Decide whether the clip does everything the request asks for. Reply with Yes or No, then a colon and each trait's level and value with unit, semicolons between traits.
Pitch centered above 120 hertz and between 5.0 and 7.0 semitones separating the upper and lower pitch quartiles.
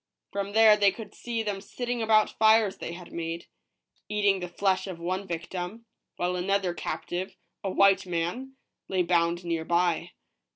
No: high, 190 Hz; average, 3.3 semitones